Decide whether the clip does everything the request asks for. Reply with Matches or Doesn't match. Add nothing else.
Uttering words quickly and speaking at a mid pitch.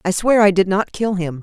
Doesn't match